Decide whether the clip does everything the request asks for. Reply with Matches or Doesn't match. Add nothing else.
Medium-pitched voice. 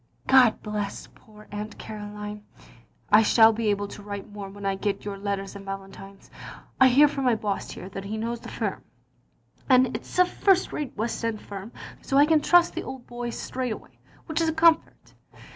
Doesn't match